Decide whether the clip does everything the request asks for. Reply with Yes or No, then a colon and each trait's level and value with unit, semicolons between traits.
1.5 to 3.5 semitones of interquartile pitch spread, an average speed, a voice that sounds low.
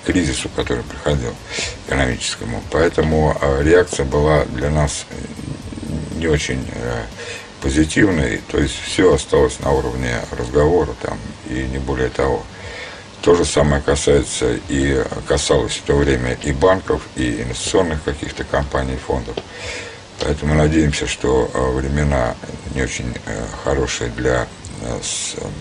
Yes: narrow, 2.5 semitones; average, 130 wpm; very low, 75 Hz